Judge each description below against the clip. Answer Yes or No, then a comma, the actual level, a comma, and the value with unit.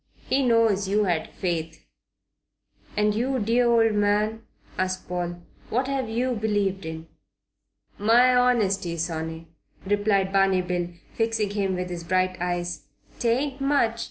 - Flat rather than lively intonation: No, average, 4.2 semitones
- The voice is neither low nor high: No, high, 205 Hz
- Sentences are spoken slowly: Yes, slow, 130 wpm